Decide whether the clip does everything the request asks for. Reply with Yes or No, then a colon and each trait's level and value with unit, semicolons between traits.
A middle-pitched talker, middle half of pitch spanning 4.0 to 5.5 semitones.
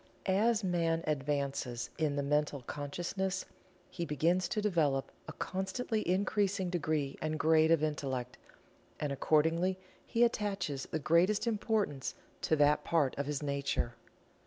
Yes: medium, 160 Hz; average, 4.8 semitones